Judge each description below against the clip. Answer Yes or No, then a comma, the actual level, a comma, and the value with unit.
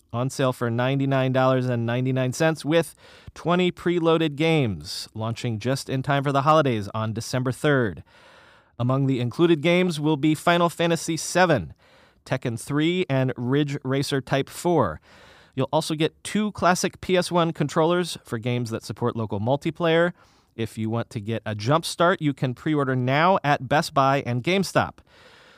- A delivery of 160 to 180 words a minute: Yes, average, 165 wpm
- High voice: No, medium, 140 Hz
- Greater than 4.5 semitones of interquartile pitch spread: Yes, average, 5.1 semitones